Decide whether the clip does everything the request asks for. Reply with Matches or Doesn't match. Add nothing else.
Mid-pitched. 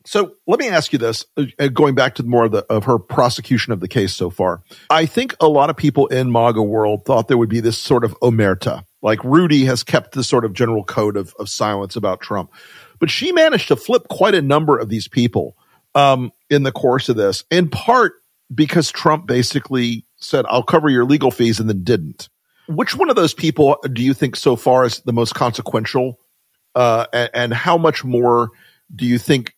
Doesn't match